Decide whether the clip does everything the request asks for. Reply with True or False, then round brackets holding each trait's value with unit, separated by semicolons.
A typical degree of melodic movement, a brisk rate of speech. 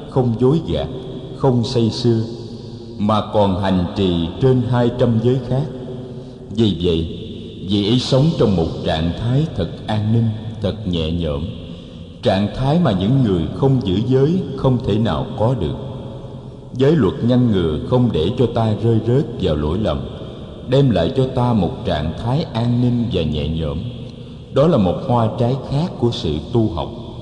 False (4.7 semitones; 175 wpm)